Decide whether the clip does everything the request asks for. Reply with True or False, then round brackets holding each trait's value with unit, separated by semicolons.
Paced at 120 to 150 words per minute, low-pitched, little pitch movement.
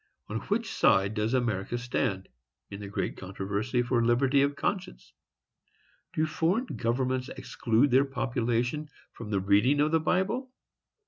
False (140 wpm; 125 Hz; 4.9 semitones)